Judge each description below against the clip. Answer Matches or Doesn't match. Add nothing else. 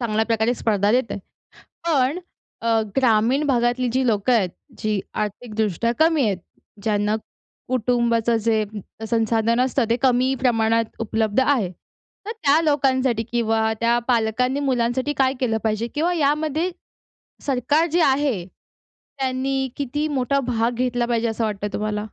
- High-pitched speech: Matches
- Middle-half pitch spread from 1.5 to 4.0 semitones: Matches